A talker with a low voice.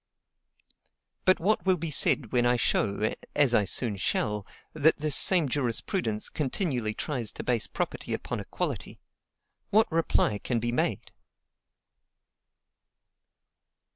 Yes: low, 125 Hz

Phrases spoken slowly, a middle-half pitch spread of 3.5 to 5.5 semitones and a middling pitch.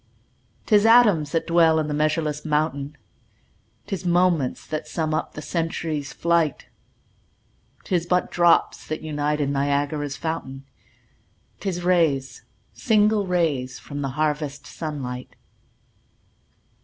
No: slow, 120 wpm; average, 3.0 semitones; medium, 155 Hz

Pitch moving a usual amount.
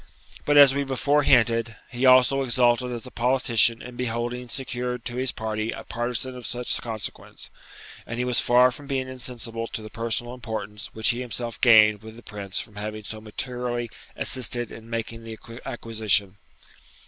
No: narrow, 2.0 semitones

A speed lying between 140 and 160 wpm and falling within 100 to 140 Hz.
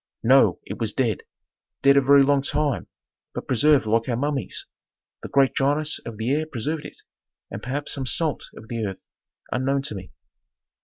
No: average, 175 wpm; low, 135 Hz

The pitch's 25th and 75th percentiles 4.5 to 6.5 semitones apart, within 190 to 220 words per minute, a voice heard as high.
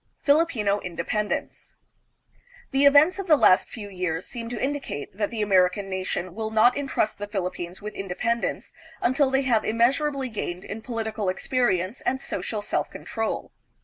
No: average, 5.3 semitones; average, 150 wpm; high, 220 Hz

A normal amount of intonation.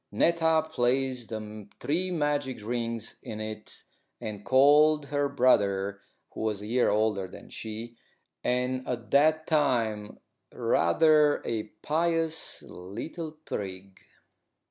No: wide, 5.8 semitones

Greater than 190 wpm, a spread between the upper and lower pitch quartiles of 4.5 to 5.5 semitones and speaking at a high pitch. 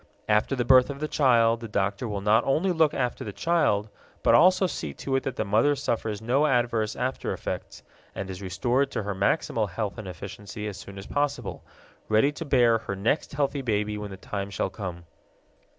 No: average, 200 wpm; average, 5.1 semitones; low, 115 Hz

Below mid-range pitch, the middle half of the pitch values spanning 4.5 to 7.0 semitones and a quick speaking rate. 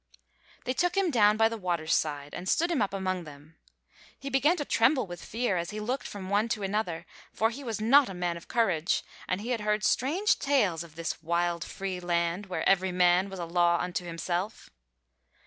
No: high, 195 Hz; average, 4.9 semitones; fast, 210 wpm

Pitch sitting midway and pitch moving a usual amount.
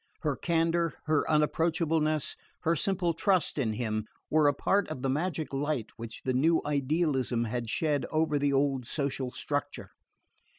Yes: medium, 150 Hz; average, 3.6 semitones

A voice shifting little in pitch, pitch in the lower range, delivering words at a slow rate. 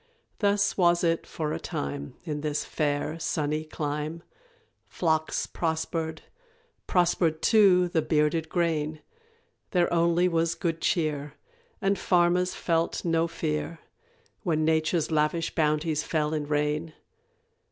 No: narrow, 2.0 semitones; medium, 160 Hz; slow, 120 wpm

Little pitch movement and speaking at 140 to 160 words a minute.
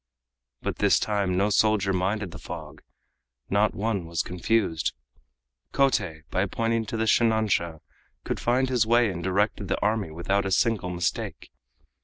No: average, 3.6 semitones; average, 150 wpm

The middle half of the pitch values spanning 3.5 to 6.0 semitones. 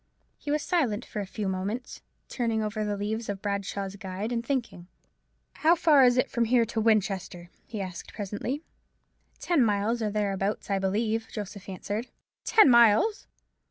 No: average, 3.1 semitones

